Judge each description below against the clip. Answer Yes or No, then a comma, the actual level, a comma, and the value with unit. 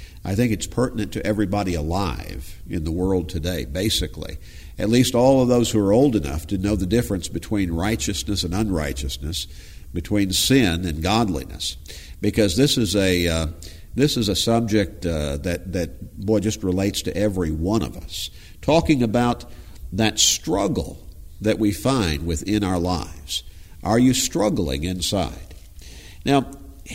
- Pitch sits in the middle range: No, very low, 95 Hz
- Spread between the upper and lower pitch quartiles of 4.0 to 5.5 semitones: Yes, average, 4.6 semitones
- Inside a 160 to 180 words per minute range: No, average, 150 wpm